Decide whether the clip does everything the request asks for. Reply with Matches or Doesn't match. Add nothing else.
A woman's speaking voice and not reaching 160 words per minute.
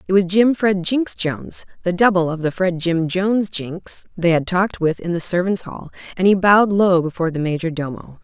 Doesn't match